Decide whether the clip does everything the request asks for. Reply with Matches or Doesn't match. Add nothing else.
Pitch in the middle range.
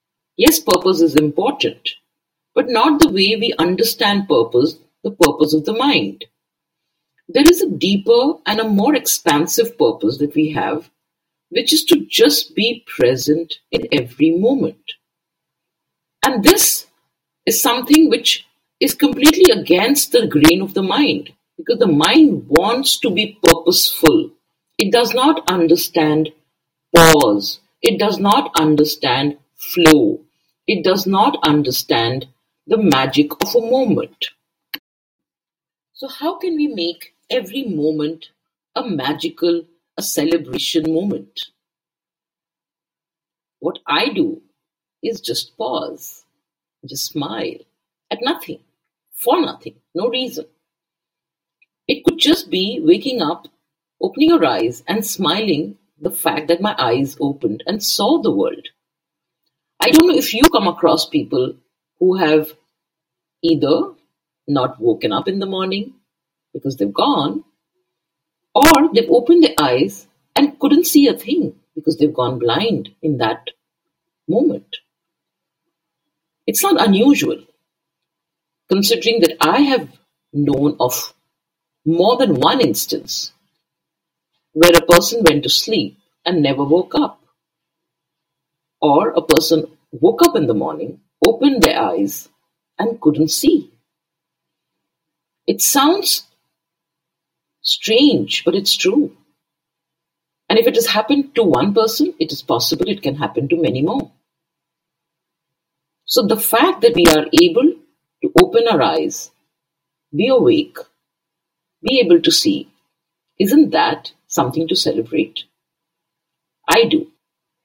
Matches